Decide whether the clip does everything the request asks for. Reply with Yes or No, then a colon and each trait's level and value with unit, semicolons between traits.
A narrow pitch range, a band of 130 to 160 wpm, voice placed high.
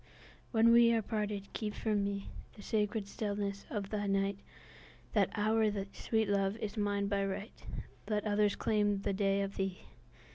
Yes: narrow, 1.4 semitones; average, 145 wpm; high, 205 Hz